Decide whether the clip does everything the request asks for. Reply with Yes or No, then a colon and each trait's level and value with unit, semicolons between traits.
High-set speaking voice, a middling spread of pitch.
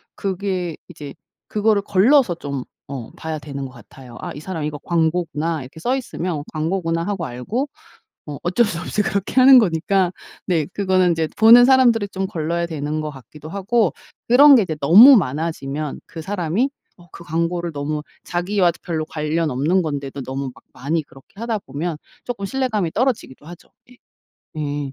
No: medium, 170 Hz; average, 5.0 semitones